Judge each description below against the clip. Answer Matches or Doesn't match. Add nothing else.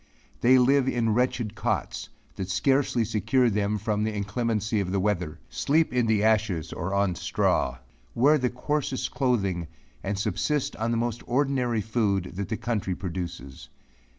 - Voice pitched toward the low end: Matches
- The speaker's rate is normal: Matches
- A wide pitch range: Doesn't match